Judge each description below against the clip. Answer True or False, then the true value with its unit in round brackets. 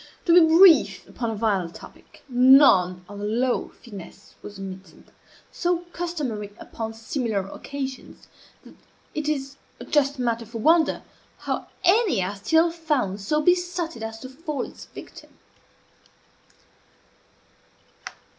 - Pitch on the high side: True (255 Hz)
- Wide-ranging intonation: True (7.4 semitones)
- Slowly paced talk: True (125 wpm)